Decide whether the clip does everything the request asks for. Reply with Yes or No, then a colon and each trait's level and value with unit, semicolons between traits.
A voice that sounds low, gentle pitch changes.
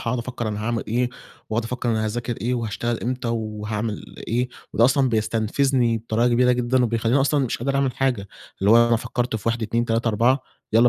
Yes: low, 120 Hz; narrow, 1.9 semitones